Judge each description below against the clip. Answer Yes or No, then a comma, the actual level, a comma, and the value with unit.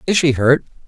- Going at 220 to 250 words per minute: No, fast, 205 wpm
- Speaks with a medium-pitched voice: Yes, medium, 145 Hz